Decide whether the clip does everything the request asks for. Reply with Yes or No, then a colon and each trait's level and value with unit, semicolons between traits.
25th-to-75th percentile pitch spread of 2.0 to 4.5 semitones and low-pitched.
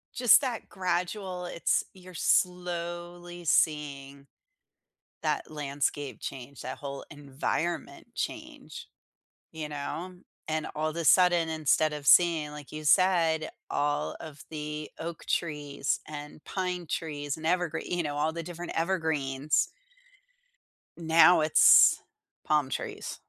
No: average, 2.9 semitones; medium, 160 Hz